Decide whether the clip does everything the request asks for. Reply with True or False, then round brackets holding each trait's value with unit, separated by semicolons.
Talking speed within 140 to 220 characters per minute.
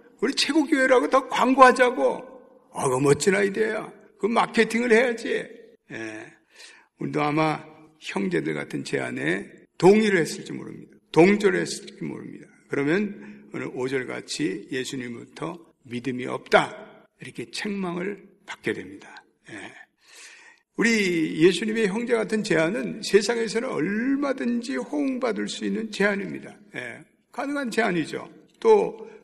False (280 characters per minute)